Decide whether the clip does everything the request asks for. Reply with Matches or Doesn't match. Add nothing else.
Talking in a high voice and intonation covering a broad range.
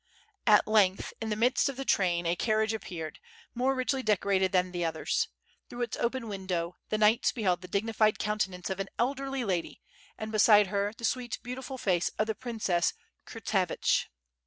Doesn't match